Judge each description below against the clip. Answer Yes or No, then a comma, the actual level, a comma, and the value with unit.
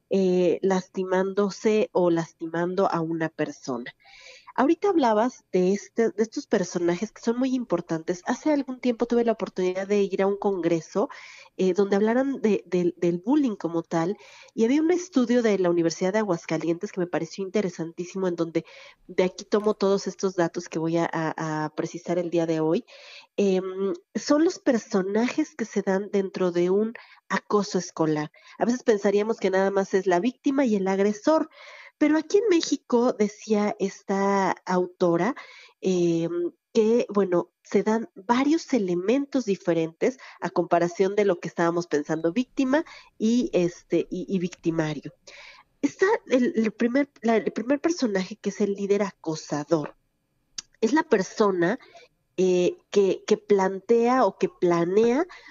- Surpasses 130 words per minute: Yes, average, 155 wpm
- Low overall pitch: No, high, 195 Hz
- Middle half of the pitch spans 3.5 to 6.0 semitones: Yes, average, 5.1 semitones